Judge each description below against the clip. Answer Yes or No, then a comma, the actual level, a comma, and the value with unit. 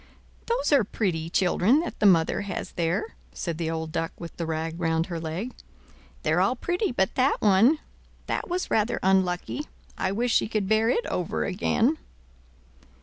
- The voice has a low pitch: No, high, 190 Hz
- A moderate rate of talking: Yes, average, 170 wpm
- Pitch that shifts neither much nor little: No, wide, 6.5 semitones